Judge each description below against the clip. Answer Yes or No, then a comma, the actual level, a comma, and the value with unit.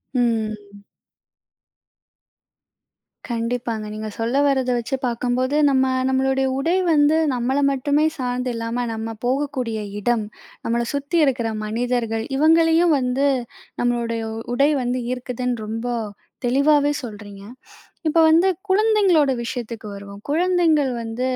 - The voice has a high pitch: Yes, very high, 250 Hz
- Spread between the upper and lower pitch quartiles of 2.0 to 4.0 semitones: Yes, average, 3.7 semitones